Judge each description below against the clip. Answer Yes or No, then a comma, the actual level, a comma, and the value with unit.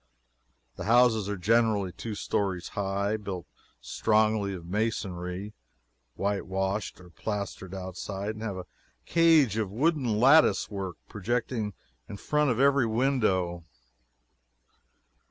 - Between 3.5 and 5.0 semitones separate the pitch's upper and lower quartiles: No, average, 3.1 semitones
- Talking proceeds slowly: Yes, slow, 115 wpm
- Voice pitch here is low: Yes, low, 105 Hz